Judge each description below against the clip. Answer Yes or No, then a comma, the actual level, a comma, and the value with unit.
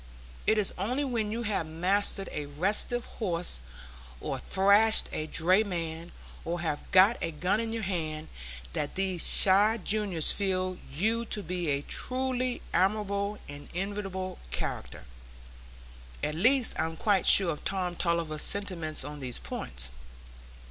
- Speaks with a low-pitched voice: No, medium, 185 Hz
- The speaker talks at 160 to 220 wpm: No, average, 140 wpm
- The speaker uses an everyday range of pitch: Yes, average, 4.3 semitones